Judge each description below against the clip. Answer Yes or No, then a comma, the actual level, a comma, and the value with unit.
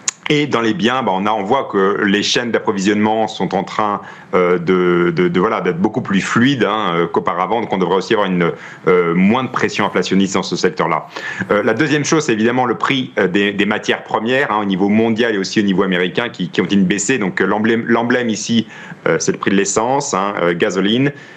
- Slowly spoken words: No, fast, 220 wpm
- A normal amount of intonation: Yes, average, 3.4 semitones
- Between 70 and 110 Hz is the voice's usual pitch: Yes, low, 105 Hz